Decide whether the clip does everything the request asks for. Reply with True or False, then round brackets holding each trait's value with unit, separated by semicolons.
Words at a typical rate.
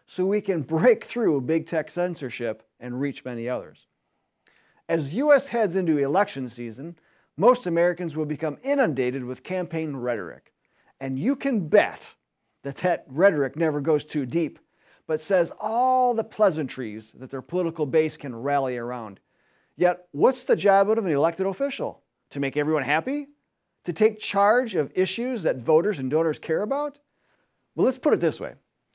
True (160 wpm)